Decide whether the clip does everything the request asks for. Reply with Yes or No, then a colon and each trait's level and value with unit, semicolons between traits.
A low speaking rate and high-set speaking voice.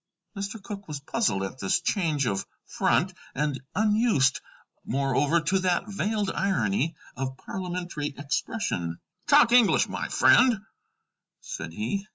No: slow, 125 wpm; medium, 170 Hz